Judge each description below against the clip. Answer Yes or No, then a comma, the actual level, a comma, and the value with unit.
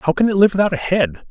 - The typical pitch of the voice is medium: Yes, medium, 175 Hz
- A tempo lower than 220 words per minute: No, fast, 320 wpm